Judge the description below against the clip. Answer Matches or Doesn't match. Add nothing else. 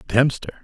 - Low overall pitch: Matches